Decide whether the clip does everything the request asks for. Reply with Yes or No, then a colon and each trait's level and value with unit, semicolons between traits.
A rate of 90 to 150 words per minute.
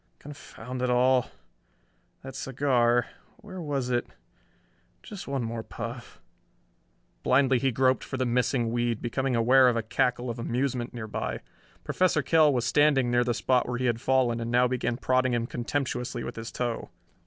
No: average, 165 wpm